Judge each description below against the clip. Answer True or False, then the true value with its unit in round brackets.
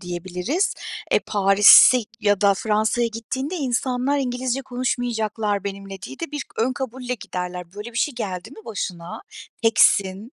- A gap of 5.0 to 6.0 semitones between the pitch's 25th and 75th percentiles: False (4.3 semitones)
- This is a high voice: True (225 Hz)